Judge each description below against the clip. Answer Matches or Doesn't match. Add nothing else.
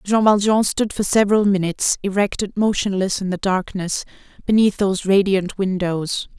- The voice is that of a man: Doesn't match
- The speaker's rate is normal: Matches